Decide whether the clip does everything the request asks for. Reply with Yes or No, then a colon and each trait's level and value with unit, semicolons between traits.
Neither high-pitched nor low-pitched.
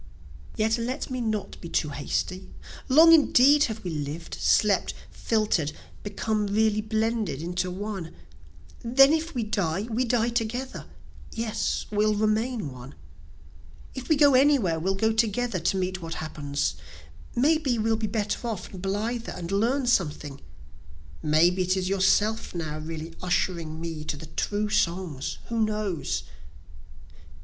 No: high, 210 Hz